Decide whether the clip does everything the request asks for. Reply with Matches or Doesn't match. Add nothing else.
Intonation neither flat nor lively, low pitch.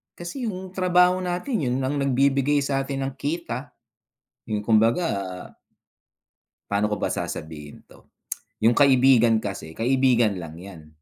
Doesn't match